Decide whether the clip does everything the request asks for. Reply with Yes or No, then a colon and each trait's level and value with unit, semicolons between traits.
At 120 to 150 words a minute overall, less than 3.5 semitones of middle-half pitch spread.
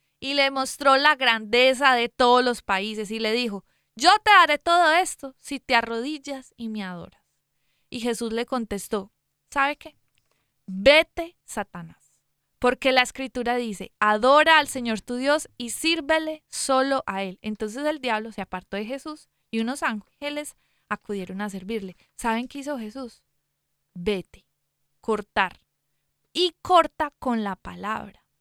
No: average, 145 wpm; average, 5.1 semitones